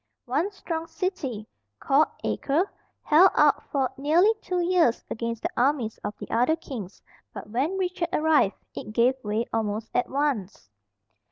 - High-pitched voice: Yes, very high, 275 Hz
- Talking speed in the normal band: Yes, average, 150 wpm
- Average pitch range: No, wide, 6.4 semitones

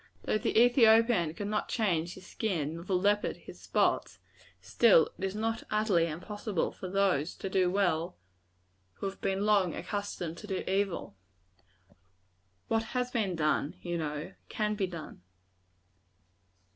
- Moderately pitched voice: No, high, 195 Hz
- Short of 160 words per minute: Yes, average, 145 wpm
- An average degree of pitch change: Yes, average, 3.8 semitones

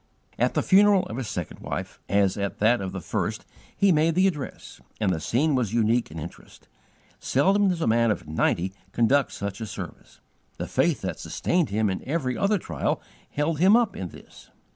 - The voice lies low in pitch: Yes, low, 120 Hz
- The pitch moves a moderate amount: No, wide, 8.9 semitones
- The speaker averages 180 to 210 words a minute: Yes, average, 195 wpm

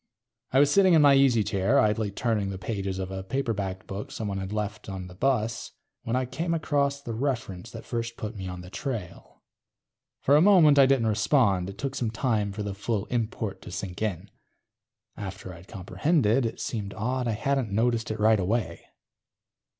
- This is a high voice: No, low, 110 Hz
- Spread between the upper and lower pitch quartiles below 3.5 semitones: No, average, 4.9 semitones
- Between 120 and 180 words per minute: No, average, 190 wpm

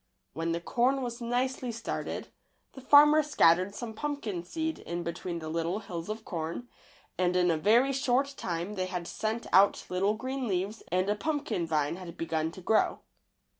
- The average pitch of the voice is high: Yes, high, 200 Hz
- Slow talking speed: No, average, 180 wpm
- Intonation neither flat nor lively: No, wide, 6.5 semitones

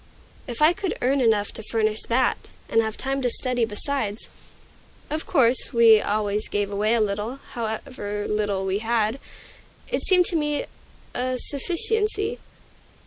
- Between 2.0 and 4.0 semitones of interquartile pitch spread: No, average, 4.7 semitones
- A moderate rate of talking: Yes, average, 145 wpm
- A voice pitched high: Yes, high, 235 Hz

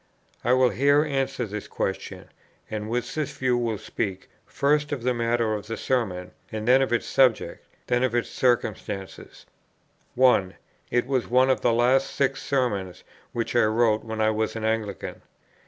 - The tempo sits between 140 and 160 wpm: No, average, 170 wpm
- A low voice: Yes, low, 120 Hz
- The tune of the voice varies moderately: Yes, average, 3.1 semitones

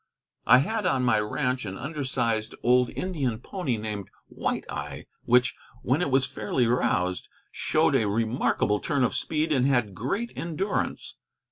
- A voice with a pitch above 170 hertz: No, low, 125 Hz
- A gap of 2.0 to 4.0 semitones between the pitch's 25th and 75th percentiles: No, average, 4.8 semitones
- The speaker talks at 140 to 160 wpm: Yes, average, 155 wpm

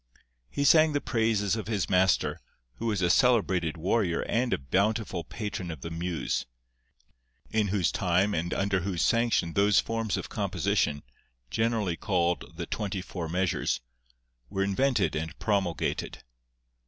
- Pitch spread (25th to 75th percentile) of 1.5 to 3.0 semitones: No, average, 4.4 semitones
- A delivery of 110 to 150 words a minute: Yes, average, 140 wpm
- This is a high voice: No, very low, 95 Hz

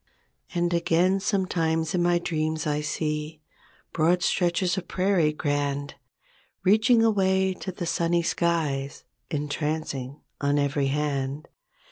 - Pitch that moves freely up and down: No, average, 3.3 semitones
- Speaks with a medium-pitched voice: Yes, medium, 160 Hz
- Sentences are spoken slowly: Yes, slow, 115 wpm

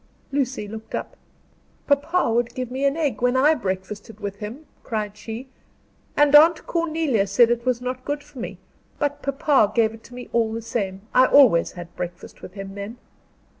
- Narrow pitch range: No, average, 5.1 semitones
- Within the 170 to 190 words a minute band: Yes, average, 185 wpm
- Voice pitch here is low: No, high, 240 Hz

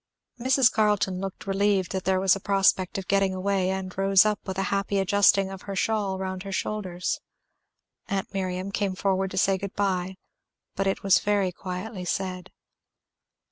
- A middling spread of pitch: No, narrow, 1.0 semitones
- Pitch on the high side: Yes, high, 195 Hz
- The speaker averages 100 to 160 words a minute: No, average, 175 wpm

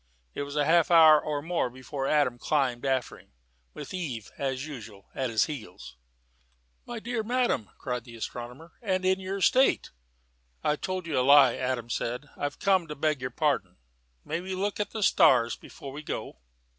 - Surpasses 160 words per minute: Yes, average, 180 wpm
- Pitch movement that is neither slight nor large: No, wide, 6.0 semitones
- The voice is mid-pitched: Yes, medium, 145 Hz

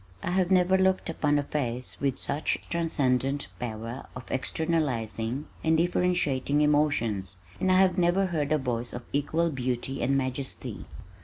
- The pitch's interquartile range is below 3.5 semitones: No, average, 5.1 semitones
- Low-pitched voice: No, medium, 145 Hz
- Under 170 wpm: Yes, average, 150 wpm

